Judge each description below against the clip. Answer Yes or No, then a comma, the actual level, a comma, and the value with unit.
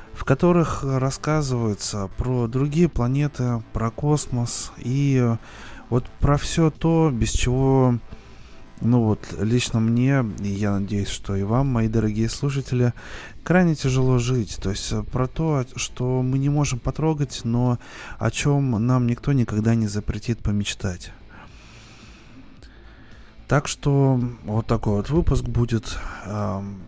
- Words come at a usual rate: Yes, average, 125 wpm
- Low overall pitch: Yes, low, 120 Hz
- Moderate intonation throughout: Yes, average, 3.7 semitones